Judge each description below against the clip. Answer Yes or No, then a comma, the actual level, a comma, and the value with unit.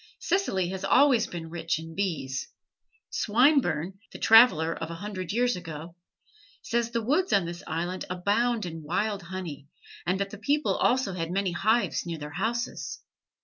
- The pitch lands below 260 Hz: Yes, high, 190 Hz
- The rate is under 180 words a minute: Yes, average, 160 wpm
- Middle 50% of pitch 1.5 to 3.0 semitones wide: No, wide, 5.6 semitones